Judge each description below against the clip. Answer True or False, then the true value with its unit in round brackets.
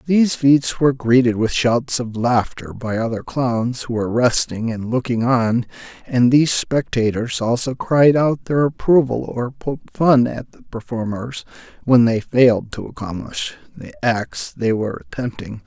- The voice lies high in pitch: False (120 Hz)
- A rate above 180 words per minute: False (155 wpm)